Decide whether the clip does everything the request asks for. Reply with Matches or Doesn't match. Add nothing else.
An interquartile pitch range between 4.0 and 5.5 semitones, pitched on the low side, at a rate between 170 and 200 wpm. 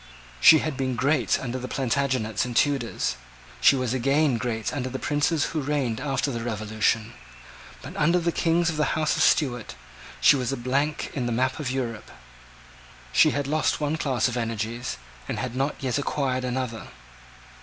Doesn't match